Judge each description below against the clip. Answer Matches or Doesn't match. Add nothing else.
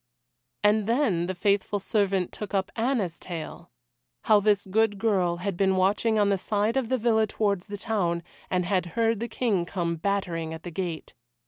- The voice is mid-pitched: Doesn't match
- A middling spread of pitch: Matches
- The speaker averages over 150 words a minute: Matches